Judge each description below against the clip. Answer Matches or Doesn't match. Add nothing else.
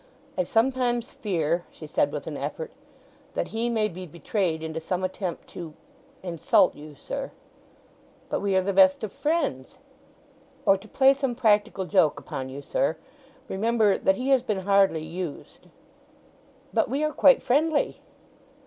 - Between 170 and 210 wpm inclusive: Doesn't match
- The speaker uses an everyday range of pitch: Doesn't match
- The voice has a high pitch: Matches